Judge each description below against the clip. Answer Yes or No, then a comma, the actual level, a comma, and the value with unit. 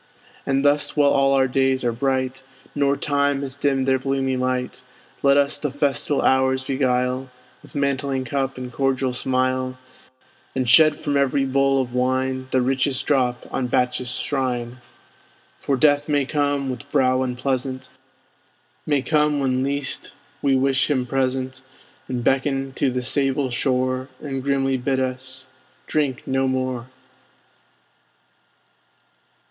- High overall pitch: No, low, 130 Hz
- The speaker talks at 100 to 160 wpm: Yes, average, 140 wpm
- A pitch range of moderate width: No, narrow, 1.4 semitones